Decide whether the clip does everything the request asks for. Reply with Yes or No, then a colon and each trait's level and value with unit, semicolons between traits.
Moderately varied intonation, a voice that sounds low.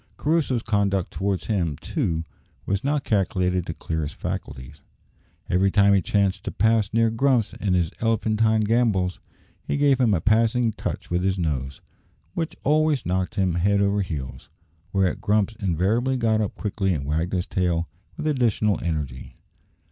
Yes: average, 4.1 semitones; low, 100 Hz